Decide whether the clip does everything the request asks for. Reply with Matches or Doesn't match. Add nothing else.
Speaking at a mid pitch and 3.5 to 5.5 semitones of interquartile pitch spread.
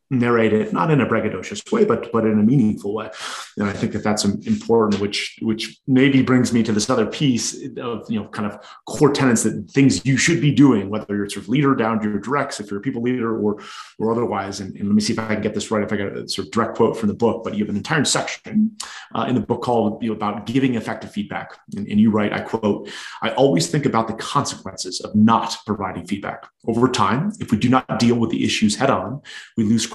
Doesn't match